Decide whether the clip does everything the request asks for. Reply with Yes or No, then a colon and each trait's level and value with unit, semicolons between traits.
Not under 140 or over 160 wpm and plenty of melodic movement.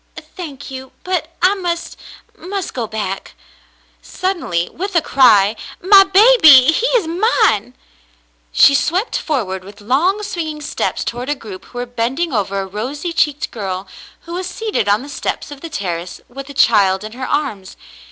No: average, 175 wpm; wide, 8.8 semitones